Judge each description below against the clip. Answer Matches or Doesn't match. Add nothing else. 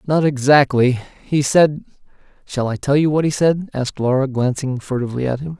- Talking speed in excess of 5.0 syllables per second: Matches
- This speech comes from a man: Matches